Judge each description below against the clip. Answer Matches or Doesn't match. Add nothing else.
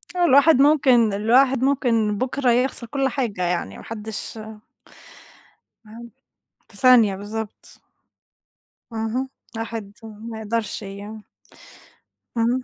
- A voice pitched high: Matches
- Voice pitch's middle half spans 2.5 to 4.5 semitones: Matches